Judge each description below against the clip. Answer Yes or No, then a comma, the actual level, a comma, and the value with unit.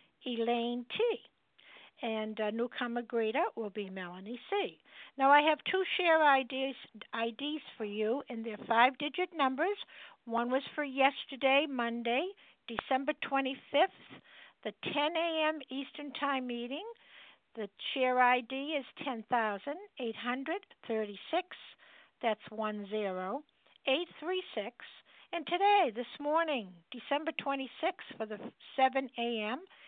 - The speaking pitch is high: Yes, very high, 265 Hz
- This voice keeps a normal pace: No, slow, 110 wpm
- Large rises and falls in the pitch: No, average, 4.6 semitones